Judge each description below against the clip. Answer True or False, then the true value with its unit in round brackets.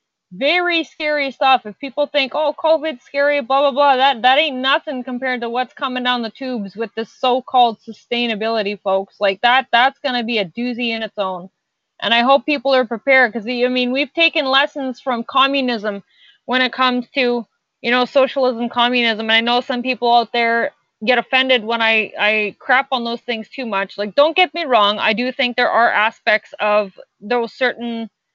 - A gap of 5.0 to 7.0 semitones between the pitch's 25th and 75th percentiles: False (3.0 semitones)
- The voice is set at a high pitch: True (250 Hz)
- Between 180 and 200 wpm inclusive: True (195 wpm)